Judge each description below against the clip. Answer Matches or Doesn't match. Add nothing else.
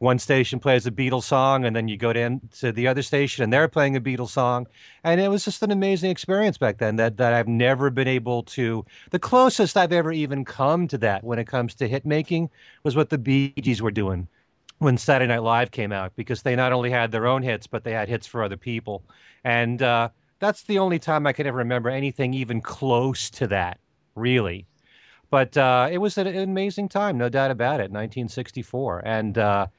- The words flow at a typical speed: Doesn't match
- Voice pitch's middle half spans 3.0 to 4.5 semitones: Matches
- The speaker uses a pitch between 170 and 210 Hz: Doesn't match